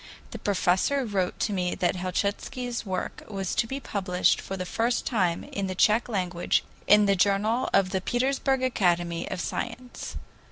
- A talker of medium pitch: No, high, 200 Hz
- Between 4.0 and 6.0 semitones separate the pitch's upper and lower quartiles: Yes, average, 4.5 semitones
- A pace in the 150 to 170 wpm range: Yes, average, 165 wpm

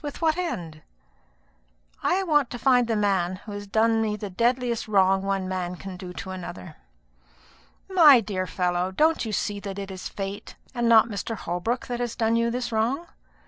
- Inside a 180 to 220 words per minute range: Yes, average, 185 wpm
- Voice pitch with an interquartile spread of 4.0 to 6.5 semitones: Yes, average, 4.3 semitones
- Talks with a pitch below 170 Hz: No, high, 215 Hz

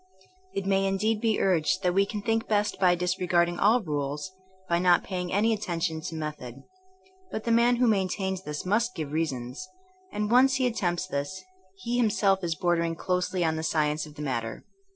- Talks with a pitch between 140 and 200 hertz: Yes, medium, 185 Hz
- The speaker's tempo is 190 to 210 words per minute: Yes, average, 195 wpm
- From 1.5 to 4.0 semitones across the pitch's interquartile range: No, average, 4.4 semitones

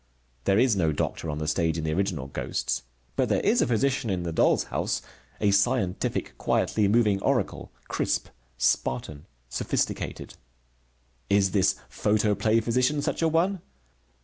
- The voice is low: Yes, low, 100 Hz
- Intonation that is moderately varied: No, wide, 6.2 semitones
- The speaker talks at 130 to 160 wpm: Yes, average, 150 wpm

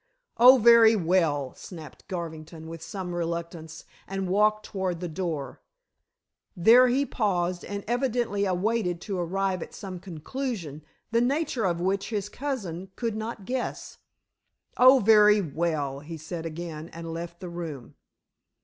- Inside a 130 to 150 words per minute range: Yes, average, 140 wpm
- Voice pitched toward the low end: No, medium, 185 Hz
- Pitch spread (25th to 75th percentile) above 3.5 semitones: Yes, average, 4.6 semitones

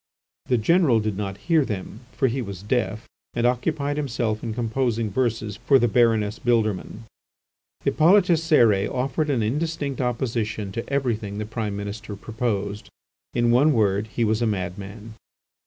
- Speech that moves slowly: No, average, 150 wpm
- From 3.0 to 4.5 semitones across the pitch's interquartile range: Yes, average, 3.7 semitones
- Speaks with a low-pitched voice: Yes, low, 115 Hz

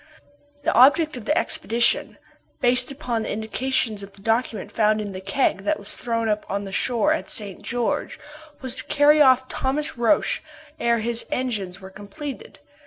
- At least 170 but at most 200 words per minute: Yes, average, 175 wpm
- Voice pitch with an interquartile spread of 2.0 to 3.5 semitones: No, average, 4.0 semitones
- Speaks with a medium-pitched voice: No, high, 235 Hz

